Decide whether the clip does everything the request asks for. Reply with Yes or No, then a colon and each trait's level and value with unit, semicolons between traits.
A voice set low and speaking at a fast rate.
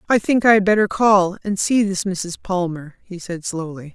No: high, 190 Hz; fast, 215 wpm